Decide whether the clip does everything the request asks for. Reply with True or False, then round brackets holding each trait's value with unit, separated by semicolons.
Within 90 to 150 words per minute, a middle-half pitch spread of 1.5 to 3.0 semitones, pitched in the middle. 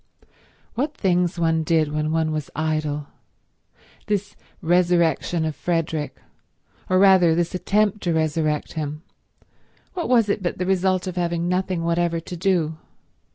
True (140 wpm; 2.7 semitones; 170 Hz)